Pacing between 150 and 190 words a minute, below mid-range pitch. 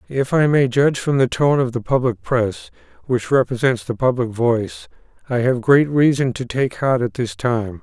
No: average, 200 wpm; low, 125 Hz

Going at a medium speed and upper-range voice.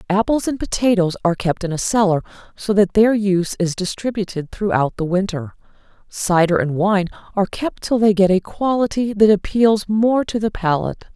Yes: average, 180 wpm; high, 200 Hz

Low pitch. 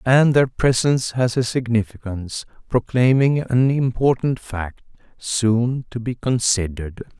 Yes: low, 120 Hz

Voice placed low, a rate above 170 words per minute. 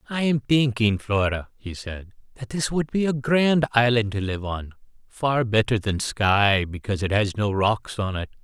Yes: low, 115 Hz; average, 185 wpm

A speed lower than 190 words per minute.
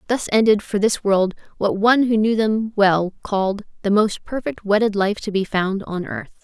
No: fast, 205 wpm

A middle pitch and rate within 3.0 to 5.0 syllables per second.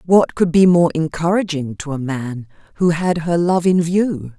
Yes: medium, 165 Hz; 4.4 syllables/s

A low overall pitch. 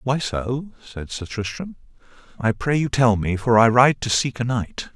Yes: low, 120 Hz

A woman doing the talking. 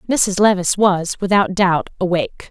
Yes: female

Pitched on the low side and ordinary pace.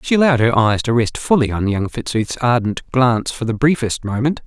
No: low, 125 Hz; fast, 215 wpm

